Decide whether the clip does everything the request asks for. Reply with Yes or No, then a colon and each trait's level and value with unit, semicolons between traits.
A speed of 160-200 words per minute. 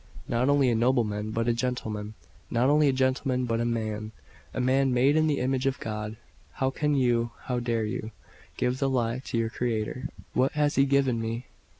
Yes: average, 195 wpm